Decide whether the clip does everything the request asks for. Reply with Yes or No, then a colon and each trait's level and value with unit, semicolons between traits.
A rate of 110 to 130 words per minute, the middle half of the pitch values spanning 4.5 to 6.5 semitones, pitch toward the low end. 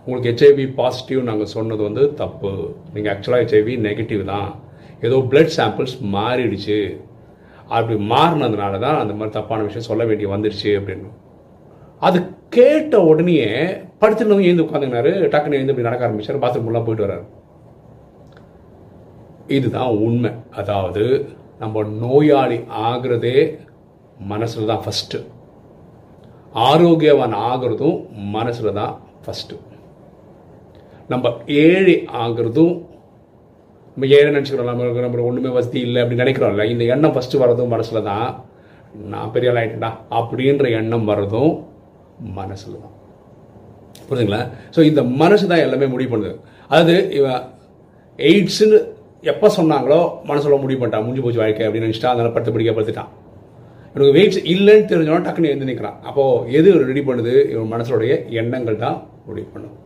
Yes: average, 125 wpm; average, 5.1 semitones; low, 120 Hz